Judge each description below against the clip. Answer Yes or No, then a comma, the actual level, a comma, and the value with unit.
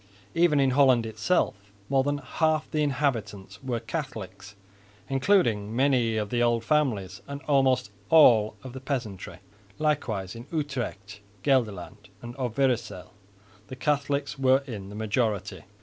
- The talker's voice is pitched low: Yes, low, 125 Hz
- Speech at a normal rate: No, slow, 130 wpm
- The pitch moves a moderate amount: Yes, average, 4.9 semitones